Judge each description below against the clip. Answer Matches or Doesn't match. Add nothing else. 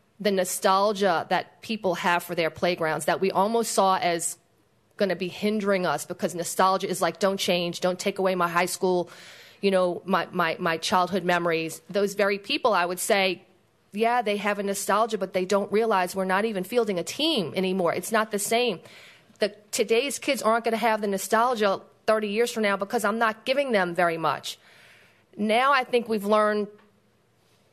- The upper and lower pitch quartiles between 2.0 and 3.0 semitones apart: Doesn't match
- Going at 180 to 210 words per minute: Matches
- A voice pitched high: Matches